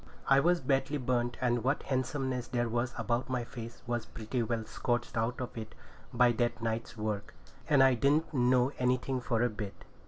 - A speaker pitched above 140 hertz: No, low, 120 Hz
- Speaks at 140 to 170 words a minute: No, average, 185 wpm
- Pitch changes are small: Yes, narrow, 1.8 semitones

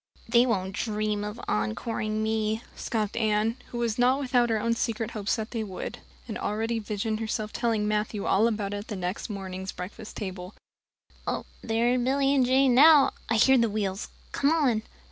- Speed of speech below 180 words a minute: No, average, 185 wpm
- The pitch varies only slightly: Yes, narrow, 2.3 semitones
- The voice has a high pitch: Yes, high, 220 Hz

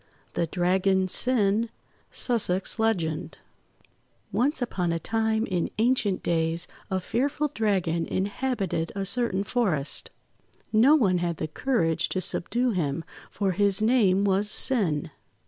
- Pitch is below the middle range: No, high, 195 Hz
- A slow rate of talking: Yes, slow, 125 wpm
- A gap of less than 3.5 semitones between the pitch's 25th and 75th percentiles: No, average, 4.6 semitones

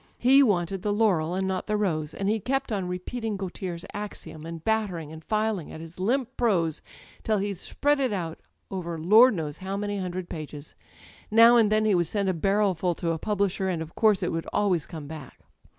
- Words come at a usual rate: No, fast, 210 wpm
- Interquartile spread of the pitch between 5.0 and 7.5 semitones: No, average, 4.3 semitones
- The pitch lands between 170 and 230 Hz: Yes, high, 190 Hz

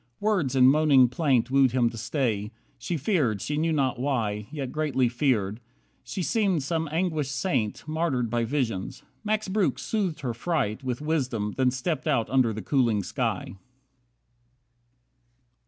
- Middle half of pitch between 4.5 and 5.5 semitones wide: Yes, average, 4.9 semitones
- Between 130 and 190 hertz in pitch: Yes, low, 135 Hz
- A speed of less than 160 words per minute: Yes, average, 150 wpm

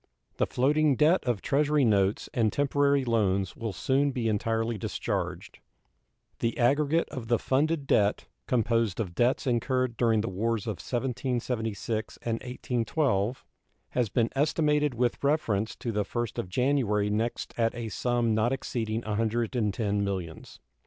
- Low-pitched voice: Yes, low, 120 Hz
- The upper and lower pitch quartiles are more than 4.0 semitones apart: No, average, 3.4 semitones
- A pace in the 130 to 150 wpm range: Yes, average, 140 wpm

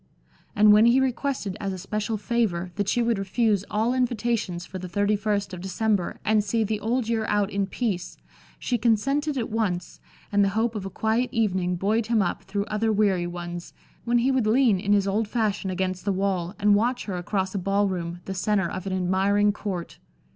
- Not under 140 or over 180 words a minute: No, fast, 205 wpm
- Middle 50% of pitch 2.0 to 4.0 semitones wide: Yes, average, 2.9 semitones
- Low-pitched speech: No, high, 205 Hz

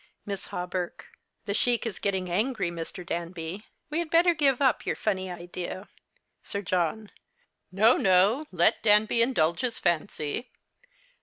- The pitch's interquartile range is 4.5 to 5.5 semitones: Yes, average, 4.8 semitones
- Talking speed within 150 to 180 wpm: No, average, 140 wpm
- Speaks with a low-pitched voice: No, high, 195 Hz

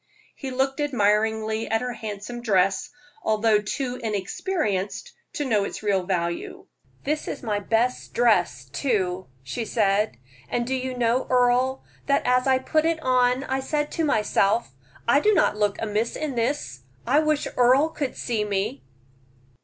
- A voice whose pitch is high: Yes, high, 235 Hz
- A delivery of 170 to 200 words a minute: No, average, 155 wpm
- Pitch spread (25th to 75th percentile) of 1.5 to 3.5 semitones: No, average, 4.2 semitones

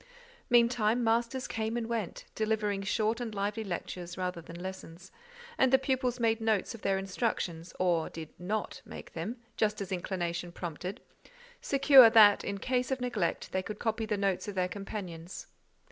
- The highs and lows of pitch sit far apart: No, average, 4.0 semitones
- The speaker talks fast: No, average, 160 wpm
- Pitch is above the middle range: Yes, high, 210 Hz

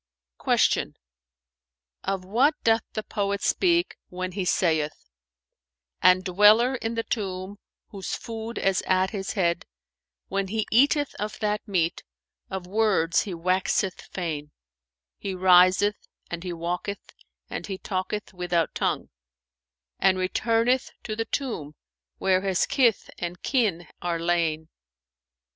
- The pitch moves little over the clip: No, average, 3.5 semitones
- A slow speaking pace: Yes, slow, 130 wpm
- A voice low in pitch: No, high, 190 Hz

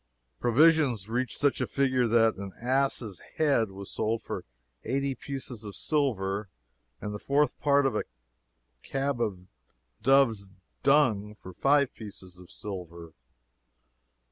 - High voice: No, low, 115 Hz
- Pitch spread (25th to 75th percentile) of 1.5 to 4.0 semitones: No, wide, 5.4 semitones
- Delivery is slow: Yes, slow, 130 wpm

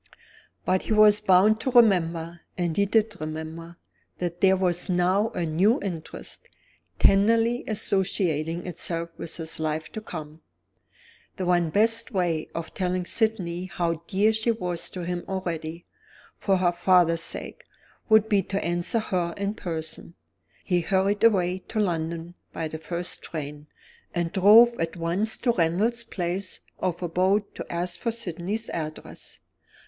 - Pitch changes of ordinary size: Yes, average, 3.5 semitones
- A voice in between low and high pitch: Yes, medium, 180 Hz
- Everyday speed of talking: Yes, average, 145 wpm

